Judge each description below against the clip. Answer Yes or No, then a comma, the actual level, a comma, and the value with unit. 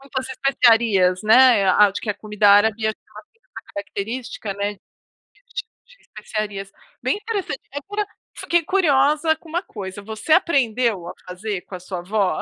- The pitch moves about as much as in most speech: No, wide, 6.0 semitones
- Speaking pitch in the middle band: No, high, 220 Hz